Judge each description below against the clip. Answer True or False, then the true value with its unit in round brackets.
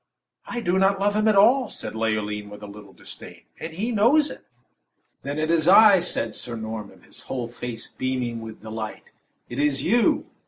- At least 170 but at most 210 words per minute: True (190 wpm)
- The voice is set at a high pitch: False (135 Hz)